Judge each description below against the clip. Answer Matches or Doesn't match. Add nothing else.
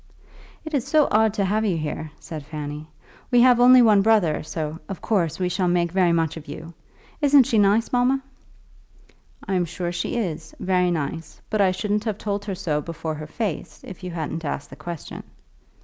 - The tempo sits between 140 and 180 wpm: Doesn't match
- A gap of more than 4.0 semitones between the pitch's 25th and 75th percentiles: Matches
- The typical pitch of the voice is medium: Matches